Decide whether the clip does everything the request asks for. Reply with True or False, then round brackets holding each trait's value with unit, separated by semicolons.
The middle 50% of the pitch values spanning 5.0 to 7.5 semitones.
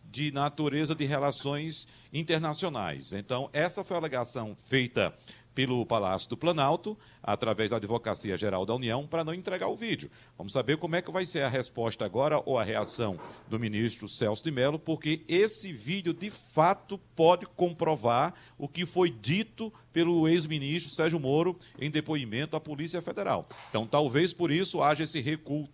True (5.3 semitones)